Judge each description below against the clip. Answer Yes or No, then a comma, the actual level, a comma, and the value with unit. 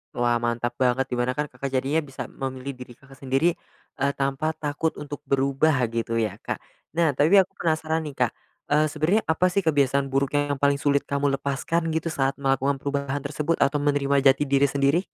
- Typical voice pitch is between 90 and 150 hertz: Yes, medium, 140 Hz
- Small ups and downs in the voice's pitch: Yes, narrow, 2.2 semitones